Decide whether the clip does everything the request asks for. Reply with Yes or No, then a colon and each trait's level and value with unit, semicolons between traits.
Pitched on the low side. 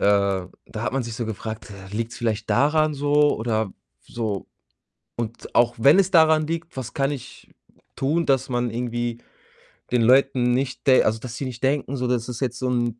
Yes: low, 120 Hz